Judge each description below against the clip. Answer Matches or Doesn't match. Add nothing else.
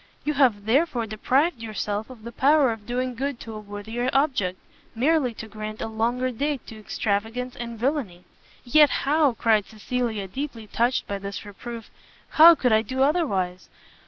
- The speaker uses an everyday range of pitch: Matches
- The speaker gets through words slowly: Doesn't match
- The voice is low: Doesn't match